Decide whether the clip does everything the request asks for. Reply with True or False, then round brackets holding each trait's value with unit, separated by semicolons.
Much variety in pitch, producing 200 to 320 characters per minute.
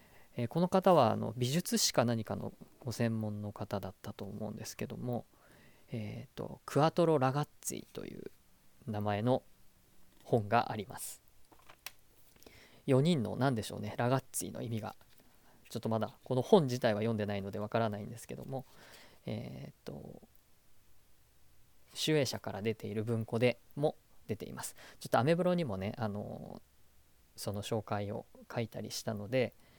False (3.5 semitones; 280 characters per minute)